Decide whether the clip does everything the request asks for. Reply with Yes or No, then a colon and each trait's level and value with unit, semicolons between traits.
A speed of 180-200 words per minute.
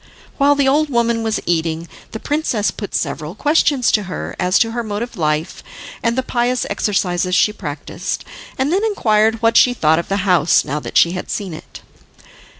Yes: average, 190 wpm